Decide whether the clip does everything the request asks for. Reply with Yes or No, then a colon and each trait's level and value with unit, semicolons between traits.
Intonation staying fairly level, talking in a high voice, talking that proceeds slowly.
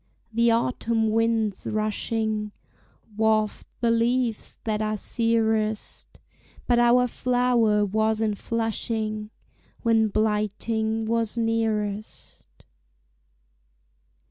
Yes: narrow, 1.3 semitones; high, 220 Hz; slow, 85 wpm